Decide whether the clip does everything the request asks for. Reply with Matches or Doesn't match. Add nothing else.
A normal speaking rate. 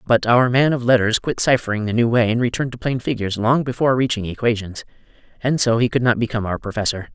Doesn't match